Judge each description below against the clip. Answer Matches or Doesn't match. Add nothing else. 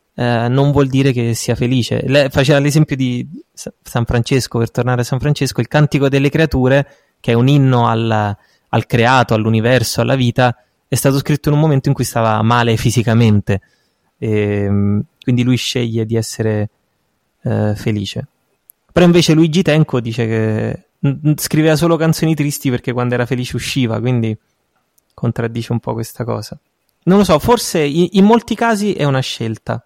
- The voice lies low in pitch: Matches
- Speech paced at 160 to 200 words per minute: Matches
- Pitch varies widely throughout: Doesn't match